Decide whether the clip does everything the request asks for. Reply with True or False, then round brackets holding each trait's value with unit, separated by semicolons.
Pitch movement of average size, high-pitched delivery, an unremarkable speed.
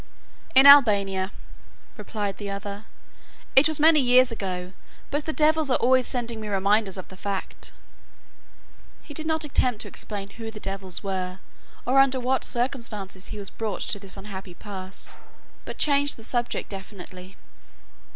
True (5.0 semitones; 210 Hz; 155 wpm)